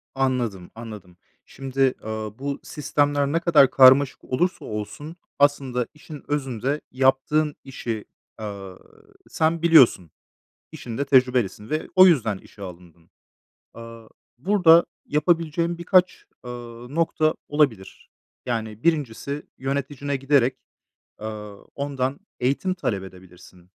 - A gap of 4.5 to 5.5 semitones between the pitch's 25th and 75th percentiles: Yes, average, 5.2 semitones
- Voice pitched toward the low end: Yes, low, 130 Hz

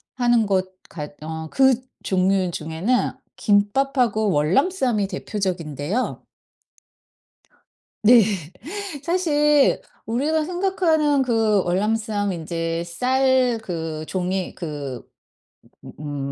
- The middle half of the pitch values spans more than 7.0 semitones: Yes, wide, 7.4 semitones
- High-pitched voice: Yes, high, 205 Hz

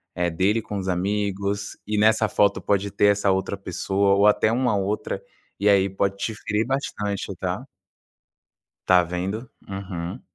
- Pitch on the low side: Yes, low, 100 Hz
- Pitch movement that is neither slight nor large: No, narrow, 1.5 semitones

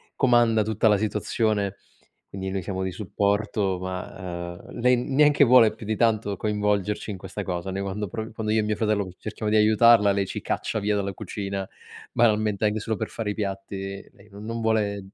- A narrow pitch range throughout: Yes, narrow, 2.0 semitones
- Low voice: Yes, low, 105 Hz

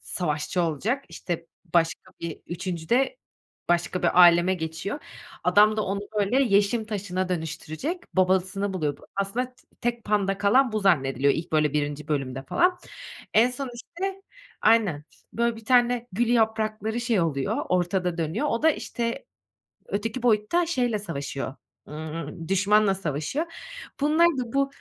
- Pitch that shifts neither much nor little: No, wide, 6.3 semitones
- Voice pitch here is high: Yes, high, 200 Hz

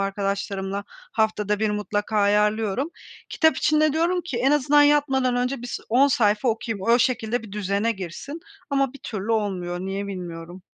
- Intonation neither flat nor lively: Yes, average, 4.9 semitones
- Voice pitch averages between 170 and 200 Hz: No, high, 220 Hz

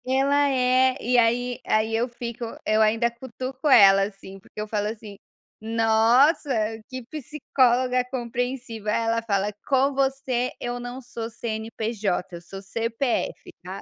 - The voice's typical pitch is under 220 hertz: No, high, 235 Hz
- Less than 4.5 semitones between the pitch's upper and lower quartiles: Yes, average, 2.8 semitones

